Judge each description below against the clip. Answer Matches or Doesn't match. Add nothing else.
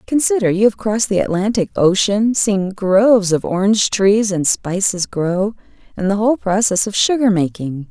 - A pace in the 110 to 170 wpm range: Matches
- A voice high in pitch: Matches